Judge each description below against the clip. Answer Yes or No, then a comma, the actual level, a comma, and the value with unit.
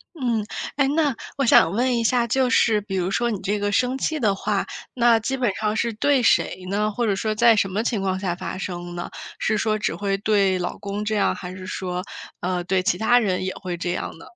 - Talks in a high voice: Yes, high, 210 Hz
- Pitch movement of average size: Yes, average, 3.9 semitones